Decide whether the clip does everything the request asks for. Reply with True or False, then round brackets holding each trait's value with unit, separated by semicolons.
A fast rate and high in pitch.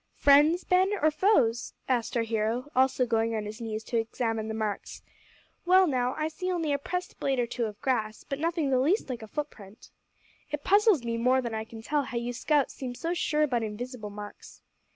True (210 wpm; 250 Hz)